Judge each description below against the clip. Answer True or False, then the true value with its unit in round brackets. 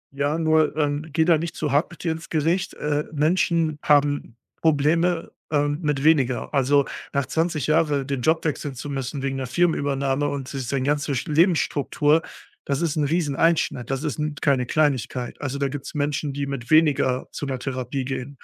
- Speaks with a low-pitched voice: False (145 Hz)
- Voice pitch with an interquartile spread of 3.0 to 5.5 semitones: False (2.4 semitones)